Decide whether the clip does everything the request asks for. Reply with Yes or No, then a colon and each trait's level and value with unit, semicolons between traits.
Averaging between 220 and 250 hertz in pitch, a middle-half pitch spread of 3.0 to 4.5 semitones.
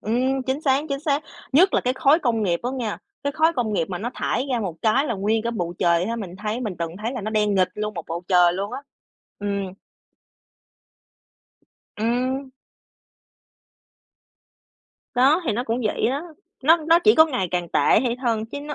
No: high, 230 Hz; average, 5.1 semitones